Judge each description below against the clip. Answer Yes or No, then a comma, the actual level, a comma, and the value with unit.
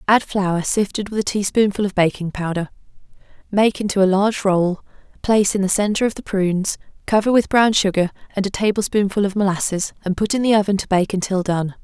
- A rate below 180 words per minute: No, average, 200 wpm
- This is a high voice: Yes, high, 200 Hz